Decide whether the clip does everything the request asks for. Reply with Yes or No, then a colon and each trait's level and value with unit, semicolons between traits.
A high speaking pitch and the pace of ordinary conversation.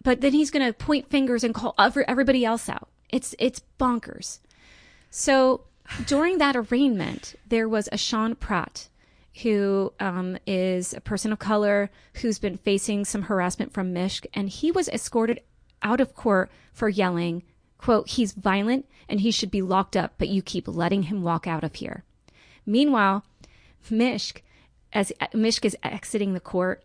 Yes: high, 215 Hz; average, 165 wpm